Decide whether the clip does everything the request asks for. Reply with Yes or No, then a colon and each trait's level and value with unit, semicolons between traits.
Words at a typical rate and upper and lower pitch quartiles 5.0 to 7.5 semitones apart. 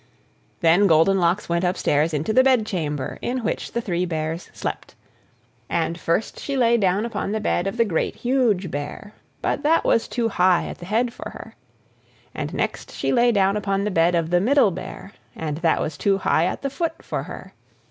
Yes: average, 195 wpm; wide, 5.4 semitones